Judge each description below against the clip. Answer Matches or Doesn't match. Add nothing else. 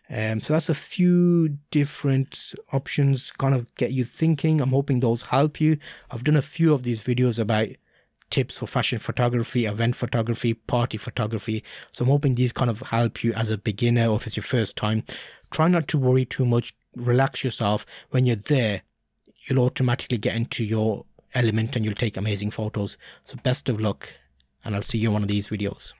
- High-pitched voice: Doesn't match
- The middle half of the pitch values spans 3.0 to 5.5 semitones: Matches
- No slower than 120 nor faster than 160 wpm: Doesn't match